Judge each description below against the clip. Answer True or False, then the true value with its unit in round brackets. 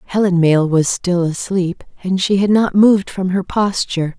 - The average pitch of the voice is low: False (185 Hz)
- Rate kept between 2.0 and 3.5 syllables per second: False (5.0 syllables/s)